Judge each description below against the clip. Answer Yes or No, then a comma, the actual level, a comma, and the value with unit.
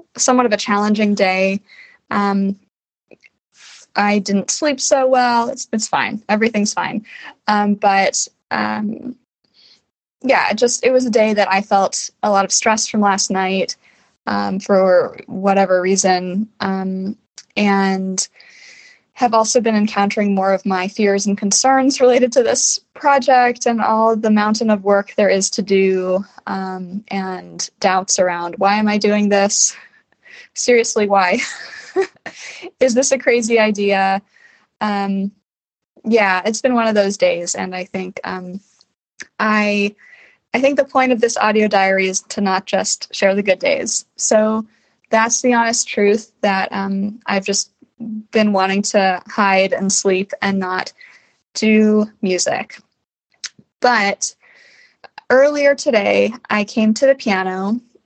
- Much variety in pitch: No, average, 3.6 semitones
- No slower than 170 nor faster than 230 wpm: No, average, 145 wpm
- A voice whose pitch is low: No, high, 210 Hz